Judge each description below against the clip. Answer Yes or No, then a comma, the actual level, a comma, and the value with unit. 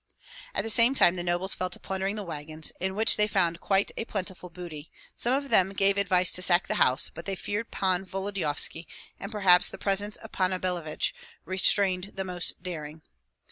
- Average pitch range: No, narrow, 2.2 semitones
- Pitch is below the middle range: No, medium, 185 Hz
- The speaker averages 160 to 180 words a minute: No, average, 195 wpm